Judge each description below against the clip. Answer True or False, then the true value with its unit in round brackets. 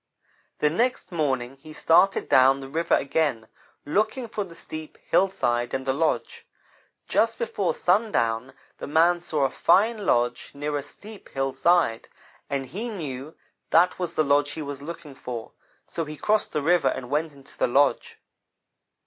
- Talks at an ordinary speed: True (160 wpm)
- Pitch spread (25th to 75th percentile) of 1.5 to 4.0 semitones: False (4.7 semitones)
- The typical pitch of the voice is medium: True (150 Hz)